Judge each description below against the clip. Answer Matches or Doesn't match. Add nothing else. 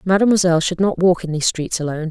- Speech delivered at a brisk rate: Matches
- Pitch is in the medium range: Matches